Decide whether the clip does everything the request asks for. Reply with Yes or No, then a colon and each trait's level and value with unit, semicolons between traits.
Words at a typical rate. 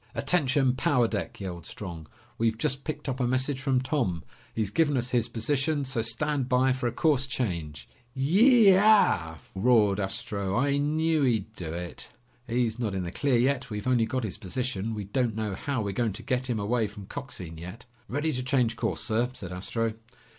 Yes: average, 190 wpm